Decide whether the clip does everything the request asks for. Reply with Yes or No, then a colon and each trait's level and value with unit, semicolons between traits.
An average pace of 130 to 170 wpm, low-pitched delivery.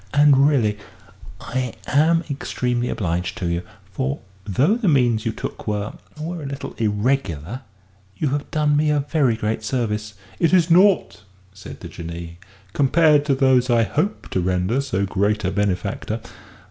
Yes: average, 160 wpm; low, 125 Hz